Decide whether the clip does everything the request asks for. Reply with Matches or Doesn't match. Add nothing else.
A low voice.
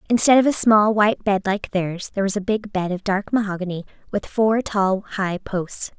Doesn't match